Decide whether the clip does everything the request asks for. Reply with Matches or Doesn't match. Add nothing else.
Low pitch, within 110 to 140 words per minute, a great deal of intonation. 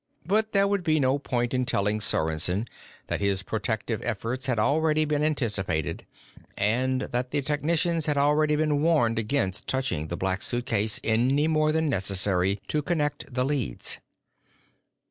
Doesn't match